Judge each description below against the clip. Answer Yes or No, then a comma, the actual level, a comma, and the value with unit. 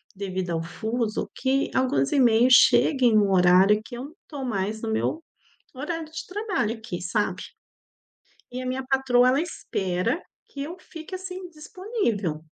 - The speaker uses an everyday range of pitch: No, wide, 6.7 semitones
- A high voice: Yes, high, 245 Hz